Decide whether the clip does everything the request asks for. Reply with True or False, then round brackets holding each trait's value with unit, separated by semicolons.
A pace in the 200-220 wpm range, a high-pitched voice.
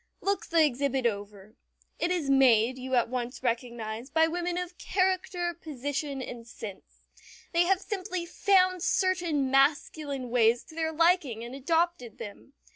False (145 wpm; 285 Hz)